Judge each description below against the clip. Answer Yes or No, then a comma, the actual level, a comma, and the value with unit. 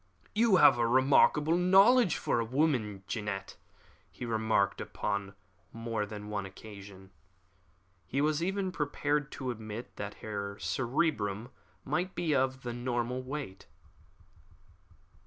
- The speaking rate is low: Yes, slow, 130 wpm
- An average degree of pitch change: No, wide, 6.2 semitones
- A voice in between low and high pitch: No, low, 120 Hz